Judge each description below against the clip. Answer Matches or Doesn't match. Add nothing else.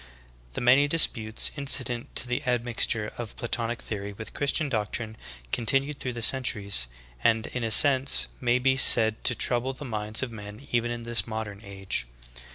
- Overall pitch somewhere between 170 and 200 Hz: Doesn't match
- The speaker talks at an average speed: Matches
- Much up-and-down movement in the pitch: Doesn't match